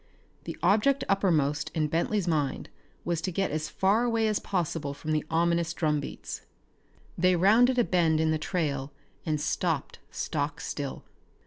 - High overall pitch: No, medium, 165 Hz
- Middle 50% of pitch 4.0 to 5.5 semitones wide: Yes, average, 4.3 semitones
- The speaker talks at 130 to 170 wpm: Yes, average, 150 wpm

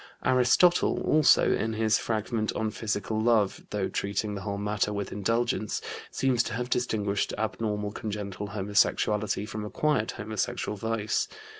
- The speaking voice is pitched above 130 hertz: No, low, 105 Hz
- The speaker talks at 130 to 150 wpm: Yes, slow, 135 wpm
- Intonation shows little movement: Yes, narrow, 1.7 semitones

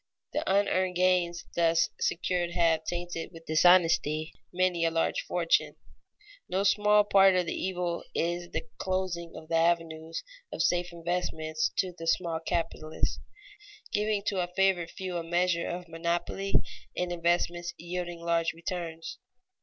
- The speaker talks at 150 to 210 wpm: No, average, 140 wpm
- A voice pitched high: No, medium, 175 Hz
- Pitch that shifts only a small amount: Yes, narrow, 1.6 semitones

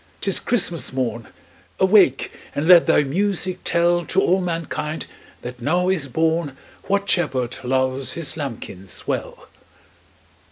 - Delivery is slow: Yes, slow, 130 wpm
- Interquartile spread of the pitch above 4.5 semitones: Yes, wide, 5.5 semitones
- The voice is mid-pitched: Yes, medium, 160 Hz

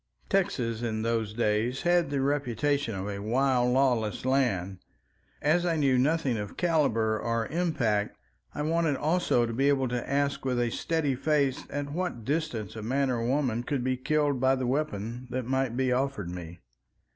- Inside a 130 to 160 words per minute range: No, average, 175 wpm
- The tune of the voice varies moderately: Yes, average, 3.9 semitones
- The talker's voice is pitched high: No, low, 130 Hz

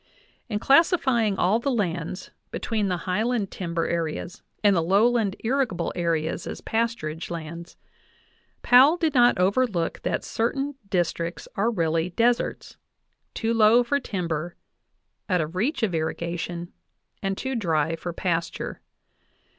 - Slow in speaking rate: Yes, slow, 130 wpm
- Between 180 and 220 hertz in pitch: Yes, high, 190 Hz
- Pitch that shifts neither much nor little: No, wide, 5.7 semitones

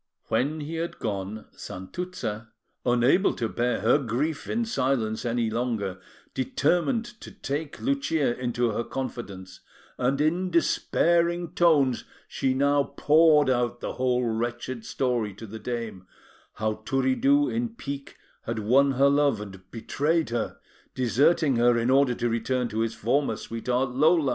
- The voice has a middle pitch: No, low, 130 Hz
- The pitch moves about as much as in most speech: Yes, average, 4.5 semitones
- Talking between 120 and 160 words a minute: Yes, average, 145 wpm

